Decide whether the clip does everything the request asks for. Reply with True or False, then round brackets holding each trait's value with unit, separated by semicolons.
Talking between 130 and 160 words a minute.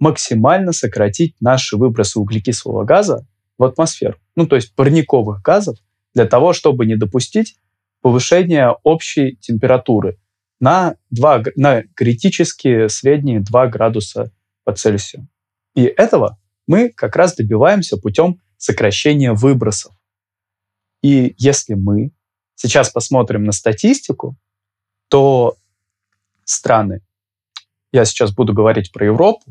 False (110 wpm)